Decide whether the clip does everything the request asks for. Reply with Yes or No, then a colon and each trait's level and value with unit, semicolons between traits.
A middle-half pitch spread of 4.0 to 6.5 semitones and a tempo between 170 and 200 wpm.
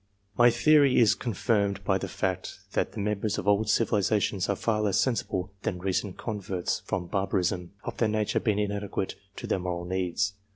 No: narrow, 2.4 semitones; average, 175 wpm